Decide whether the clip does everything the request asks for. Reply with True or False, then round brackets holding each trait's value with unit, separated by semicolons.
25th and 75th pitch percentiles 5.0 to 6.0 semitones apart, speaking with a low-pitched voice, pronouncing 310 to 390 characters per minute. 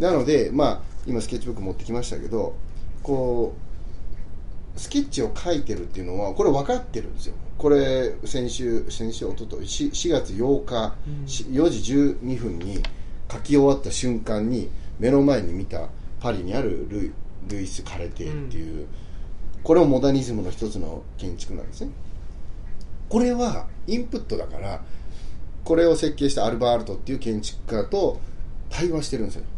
False (7.1 semitones; 110 Hz; 320 characters per minute)